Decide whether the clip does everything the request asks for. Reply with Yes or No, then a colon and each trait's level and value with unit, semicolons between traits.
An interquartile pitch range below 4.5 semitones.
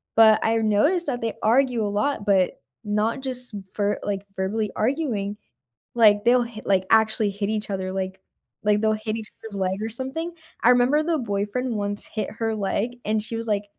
Yes: average, 2.9 semitones